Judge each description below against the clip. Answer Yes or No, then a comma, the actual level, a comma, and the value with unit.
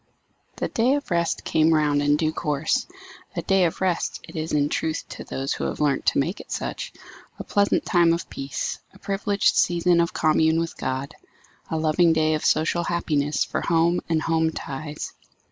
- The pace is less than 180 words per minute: No, average, 190 wpm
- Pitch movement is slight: Yes, narrow, 2.3 semitones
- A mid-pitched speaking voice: Yes, medium, 160 Hz